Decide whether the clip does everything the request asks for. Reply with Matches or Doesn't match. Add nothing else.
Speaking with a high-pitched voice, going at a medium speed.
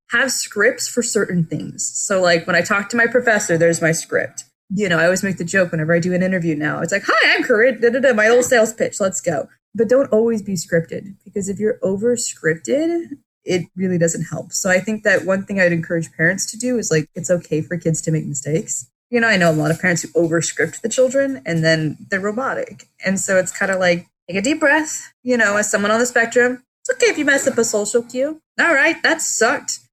Doesn't match